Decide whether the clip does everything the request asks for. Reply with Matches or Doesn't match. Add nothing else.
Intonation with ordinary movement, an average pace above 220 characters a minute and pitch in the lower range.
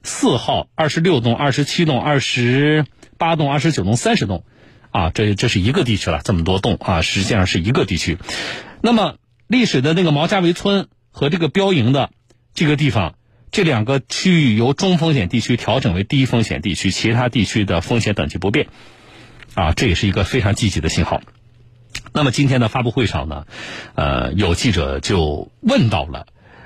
Doesn't match